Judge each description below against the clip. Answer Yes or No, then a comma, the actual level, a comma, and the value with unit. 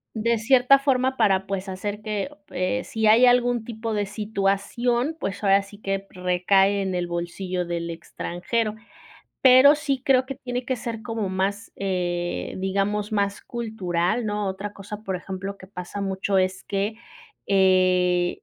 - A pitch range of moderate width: Yes, average, 3.6 semitones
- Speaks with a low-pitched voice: No, high, 200 Hz